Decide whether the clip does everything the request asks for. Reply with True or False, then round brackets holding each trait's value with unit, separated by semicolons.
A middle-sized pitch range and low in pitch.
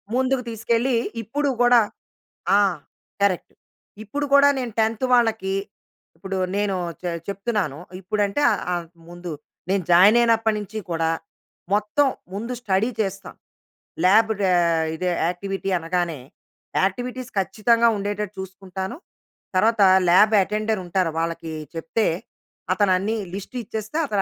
False (3.2 semitones; 205 Hz)